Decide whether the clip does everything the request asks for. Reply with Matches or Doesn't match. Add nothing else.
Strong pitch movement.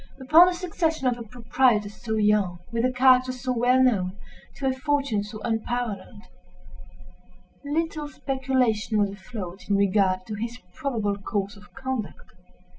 Doesn't match